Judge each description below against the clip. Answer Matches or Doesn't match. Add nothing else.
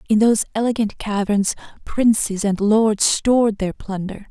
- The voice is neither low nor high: Doesn't match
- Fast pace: Doesn't match